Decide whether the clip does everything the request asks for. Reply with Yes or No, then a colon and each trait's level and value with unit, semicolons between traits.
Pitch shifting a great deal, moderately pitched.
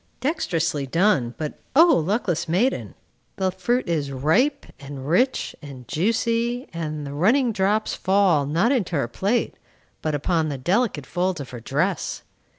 Yes: wide, 7.0 semitones; medium, 175 Hz